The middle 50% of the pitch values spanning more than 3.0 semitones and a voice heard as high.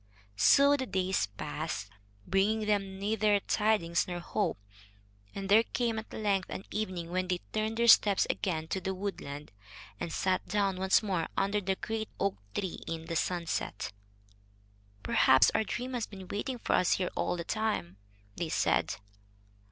Yes: average, 3.4 semitones; high, 195 Hz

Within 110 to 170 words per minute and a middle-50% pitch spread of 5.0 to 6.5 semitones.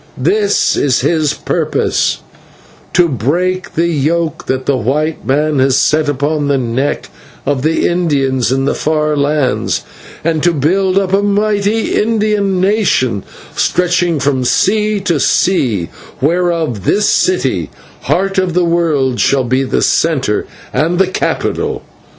Yes: average, 140 wpm; wide, 5.4 semitones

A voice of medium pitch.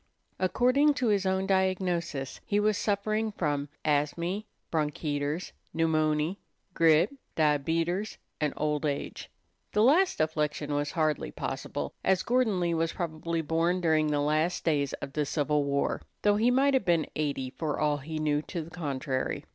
Yes: medium, 160 Hz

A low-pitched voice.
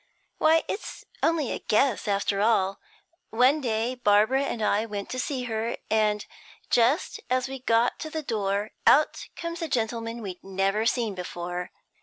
No: high, 230 Hz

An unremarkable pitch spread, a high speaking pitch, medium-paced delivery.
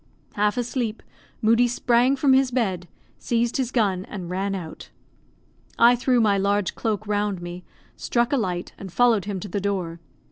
Yes: average, 4.1 semitones; high, 210 Hz; average, 170 wpm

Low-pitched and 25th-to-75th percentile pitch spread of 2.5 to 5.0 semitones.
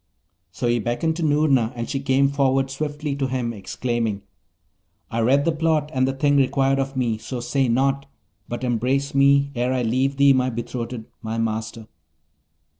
Yes: low, 130 Hz; average, 2.8 semitones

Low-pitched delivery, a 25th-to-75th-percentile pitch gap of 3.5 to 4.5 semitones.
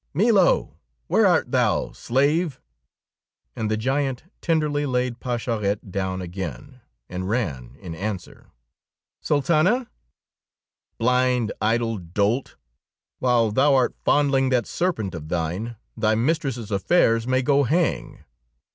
No: low, 120 Hz; wide, 5.4 semitones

